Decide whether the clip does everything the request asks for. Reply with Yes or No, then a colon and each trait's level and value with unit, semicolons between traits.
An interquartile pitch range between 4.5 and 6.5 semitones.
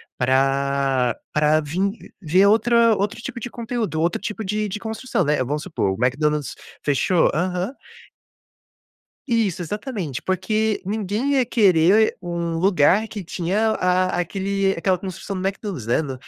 Yes: wide, 5.5 semitones